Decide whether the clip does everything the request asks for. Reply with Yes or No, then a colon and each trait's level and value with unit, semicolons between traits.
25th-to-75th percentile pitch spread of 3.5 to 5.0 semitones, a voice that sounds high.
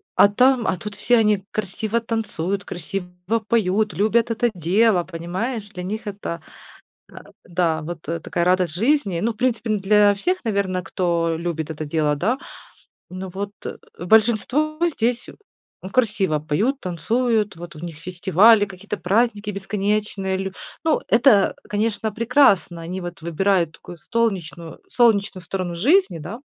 Yes: average, 4.3 semitones; high, 200 Hz